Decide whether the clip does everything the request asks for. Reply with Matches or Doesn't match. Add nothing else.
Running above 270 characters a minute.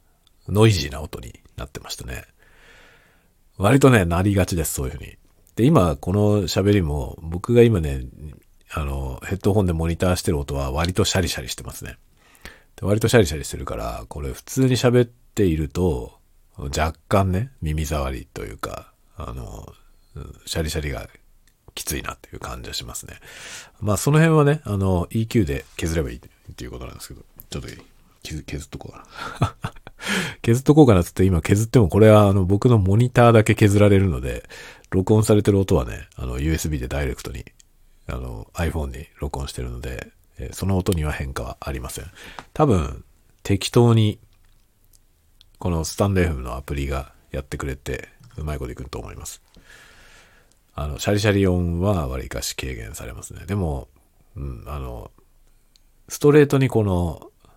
Matches